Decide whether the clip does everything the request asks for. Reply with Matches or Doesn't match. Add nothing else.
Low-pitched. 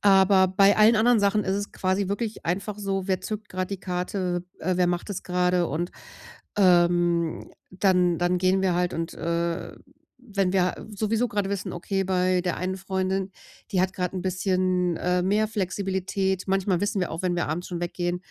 Doesn't match